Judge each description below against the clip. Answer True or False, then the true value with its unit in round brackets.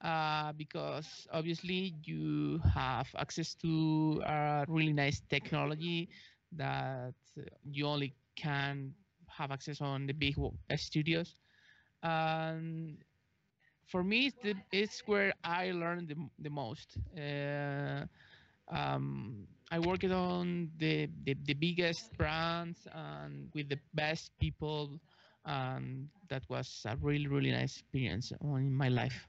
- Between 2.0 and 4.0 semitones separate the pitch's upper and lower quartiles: True (3.3 semitones)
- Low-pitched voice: False (150 Hz)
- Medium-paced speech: False (120 wpm)